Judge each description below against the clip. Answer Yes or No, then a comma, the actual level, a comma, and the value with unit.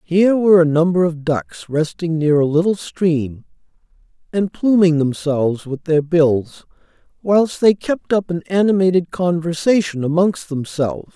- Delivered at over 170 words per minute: No, average, 140 wpm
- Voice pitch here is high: No, medium, 170 Hz